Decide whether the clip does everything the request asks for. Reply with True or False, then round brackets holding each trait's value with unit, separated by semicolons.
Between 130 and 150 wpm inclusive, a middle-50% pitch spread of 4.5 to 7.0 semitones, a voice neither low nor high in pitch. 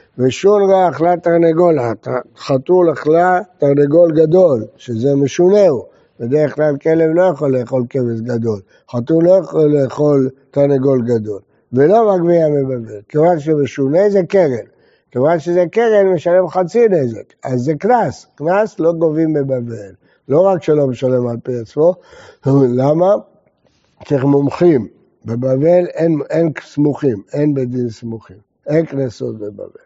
True (135 wpm; 5.2 semitones; 150 Hz)